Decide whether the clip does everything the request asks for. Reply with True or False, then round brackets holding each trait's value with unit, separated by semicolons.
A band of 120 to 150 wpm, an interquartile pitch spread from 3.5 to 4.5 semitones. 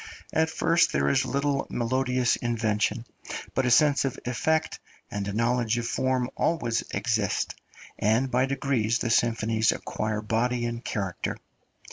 False (140 wpm; 2.8 semitones)